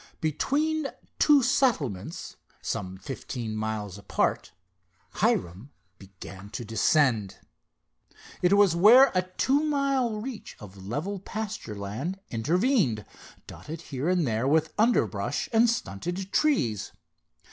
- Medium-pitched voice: Yes, medium, 160 Hz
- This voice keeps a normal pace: No, slow, 110 wpm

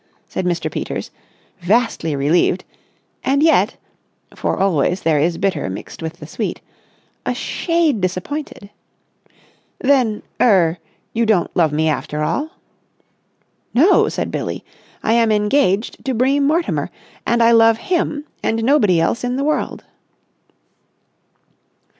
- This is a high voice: Yes, high, 220 Hz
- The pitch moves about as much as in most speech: No, wide, 7.8 semitones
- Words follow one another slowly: Yes, slow, 115 wpm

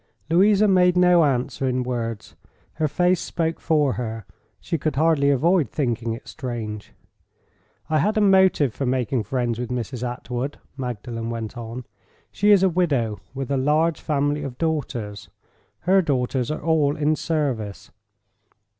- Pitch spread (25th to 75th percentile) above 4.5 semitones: Yes, average, 5.1 semitones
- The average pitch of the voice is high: No, medium, 140 Hz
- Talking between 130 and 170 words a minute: Yes, average, 150 wpm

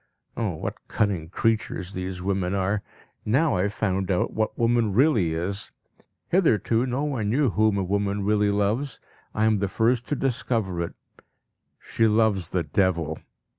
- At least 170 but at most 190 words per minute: No, average, 160 wpm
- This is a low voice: Yes, low, 105 Hz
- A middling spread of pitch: Yes, average, 3.3 semitones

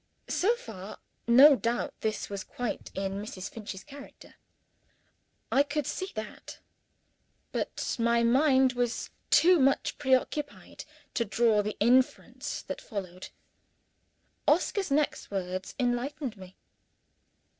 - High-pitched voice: Yes, high, 240 Hz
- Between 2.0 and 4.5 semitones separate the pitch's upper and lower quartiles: No, average, 5.2 semitones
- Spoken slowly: Yes, slow, 115 wpm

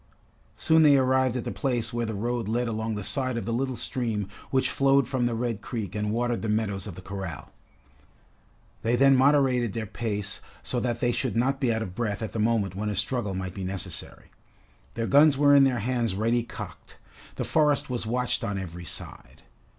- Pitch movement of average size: Yes, average, 3.6 semitones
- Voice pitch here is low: Yes, low, 115 Hz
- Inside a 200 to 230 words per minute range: Yes, fast, 205 wpm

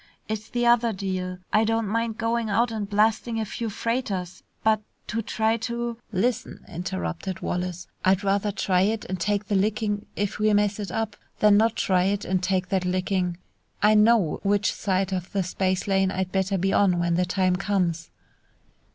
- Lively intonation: No, average, 2.9 semitones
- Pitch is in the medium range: No, high, 200 Hz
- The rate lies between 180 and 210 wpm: Yes, average, 185 wpm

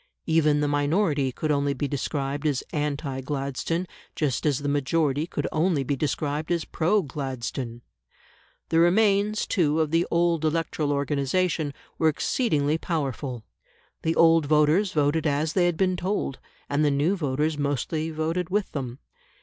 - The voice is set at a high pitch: No, medium, 150 Hz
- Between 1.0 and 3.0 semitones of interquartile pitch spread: Yes, average, 2.7 semitones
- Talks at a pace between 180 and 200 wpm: No, average, 150 wpm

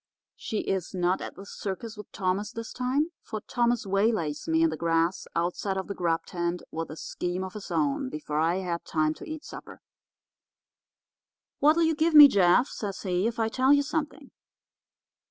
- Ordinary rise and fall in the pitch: No, wide, 5.8 semitones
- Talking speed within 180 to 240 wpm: Yes, average, 185 wpm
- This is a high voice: Yes, high, 195 Hz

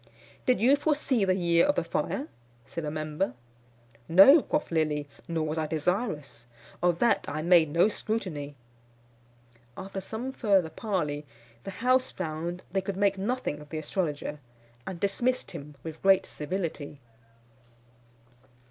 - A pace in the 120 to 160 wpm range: Yes, average, 140 wpm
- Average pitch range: Yes, average, 4.9 semitones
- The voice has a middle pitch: Yes, medium, 180 Hz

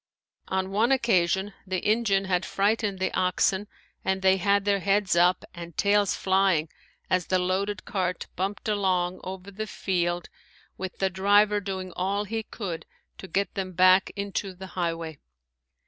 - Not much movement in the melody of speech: Yes, narrow, 1.7 semitones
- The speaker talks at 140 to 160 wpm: Yes, average, 155 wpm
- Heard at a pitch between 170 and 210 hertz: Yes, high, 190 Hz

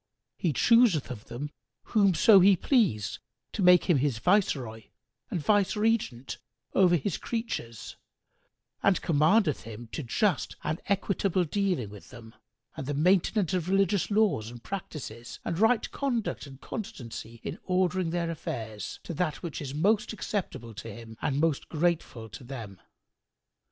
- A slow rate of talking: No, average, 145 wpm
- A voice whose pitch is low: No, medium, 165 Hz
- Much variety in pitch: Yes, wide, 8.3 semitones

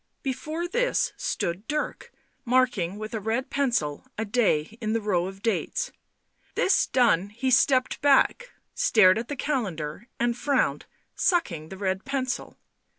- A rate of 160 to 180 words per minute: No, average, 145 wpm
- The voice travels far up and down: Yes, wide, 6.1 semitones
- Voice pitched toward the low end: No, high, 235 Hz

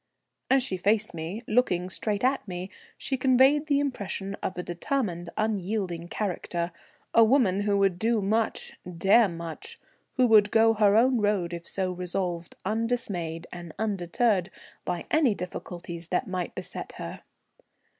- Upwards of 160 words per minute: No, average, 145 wpm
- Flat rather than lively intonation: No, average, 4.4 semitones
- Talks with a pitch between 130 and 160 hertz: No, high, 200 Hz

